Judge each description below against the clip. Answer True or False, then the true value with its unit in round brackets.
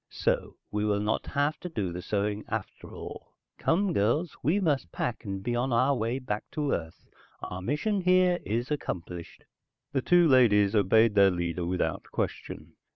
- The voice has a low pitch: True (115 Hz)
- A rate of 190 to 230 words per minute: False (170 wpm)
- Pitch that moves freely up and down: True (6.7 semitones)